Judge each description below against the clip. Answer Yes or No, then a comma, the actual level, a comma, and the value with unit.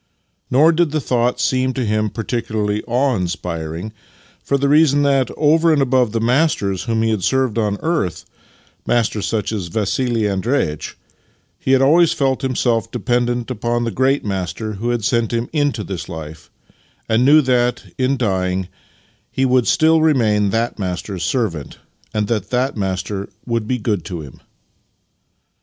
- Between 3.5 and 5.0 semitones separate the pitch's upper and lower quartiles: Yes, average, 4.2 semitones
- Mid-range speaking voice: No, low, 115 Hz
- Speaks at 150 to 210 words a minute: Yes, average, 165 wpm